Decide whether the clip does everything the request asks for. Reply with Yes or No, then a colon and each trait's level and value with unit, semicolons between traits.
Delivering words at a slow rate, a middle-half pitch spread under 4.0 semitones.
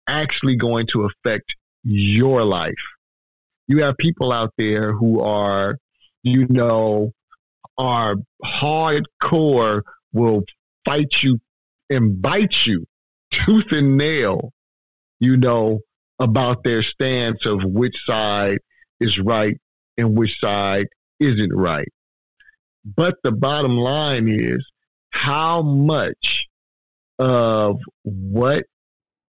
No: slow, 100 wpm; average, 4.5 semitones